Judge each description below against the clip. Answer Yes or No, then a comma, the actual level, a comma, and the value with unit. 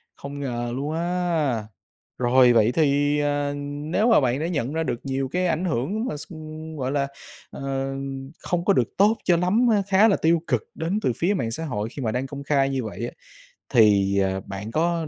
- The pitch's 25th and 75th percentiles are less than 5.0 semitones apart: No, wide, 5.4 semitones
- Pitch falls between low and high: Yes, medium, 145 Hz